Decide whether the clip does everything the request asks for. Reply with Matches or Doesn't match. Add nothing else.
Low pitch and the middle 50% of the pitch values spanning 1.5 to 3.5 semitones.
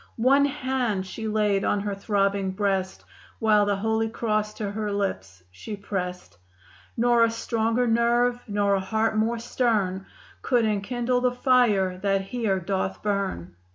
Doesn't match